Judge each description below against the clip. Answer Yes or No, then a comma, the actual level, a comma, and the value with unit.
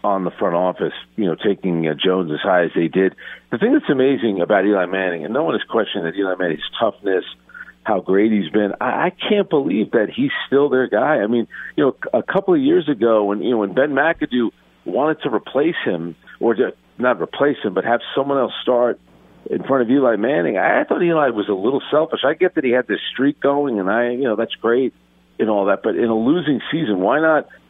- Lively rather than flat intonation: Yes, wide, 6.4 semitones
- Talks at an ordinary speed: No, fast, 230 wpm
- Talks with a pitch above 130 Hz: No, low, 115 Hz